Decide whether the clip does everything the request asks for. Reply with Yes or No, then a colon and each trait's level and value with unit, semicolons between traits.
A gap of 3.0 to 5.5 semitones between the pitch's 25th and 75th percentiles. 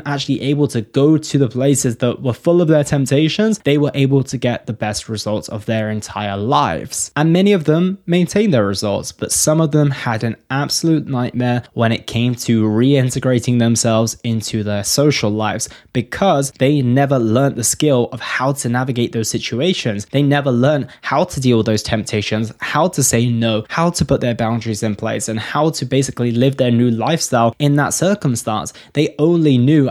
Yes: average, 4.1 semitones